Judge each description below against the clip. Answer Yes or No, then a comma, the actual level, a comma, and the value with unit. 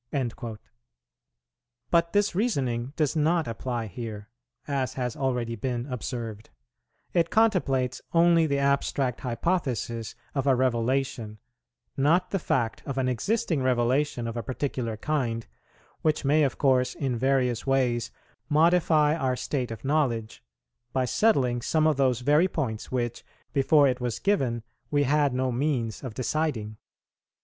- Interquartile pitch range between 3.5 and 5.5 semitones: Yes, average, 4.0 semitones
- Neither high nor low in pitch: No, low, 130 Hz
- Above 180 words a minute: No, average, 140 wpm